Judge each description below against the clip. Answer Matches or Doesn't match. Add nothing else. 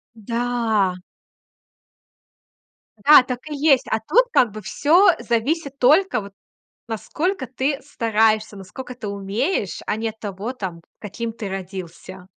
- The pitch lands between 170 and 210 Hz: Doesn't match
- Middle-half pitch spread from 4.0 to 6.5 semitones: Matches